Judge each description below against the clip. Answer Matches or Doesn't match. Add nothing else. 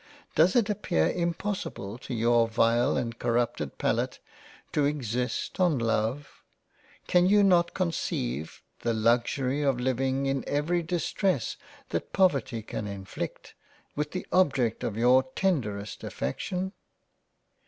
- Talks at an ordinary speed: Doesn't match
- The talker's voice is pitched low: Matches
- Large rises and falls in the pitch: Matches